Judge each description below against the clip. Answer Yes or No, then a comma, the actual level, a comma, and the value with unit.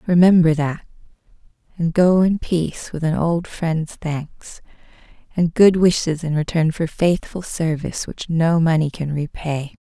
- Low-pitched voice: No, medium, 165 Hz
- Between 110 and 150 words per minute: Yes, average, 145 wpm